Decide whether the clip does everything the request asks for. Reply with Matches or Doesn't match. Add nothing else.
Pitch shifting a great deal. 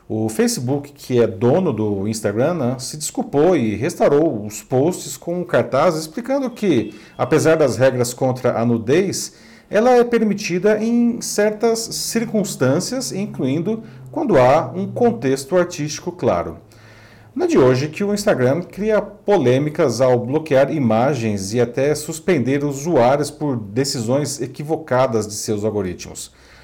Matches